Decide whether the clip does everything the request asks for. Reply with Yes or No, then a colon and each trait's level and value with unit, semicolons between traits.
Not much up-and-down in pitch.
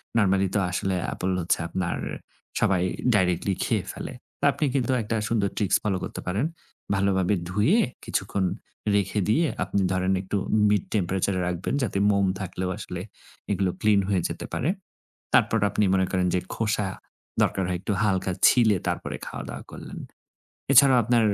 Yes: narrow, 2.2 semitones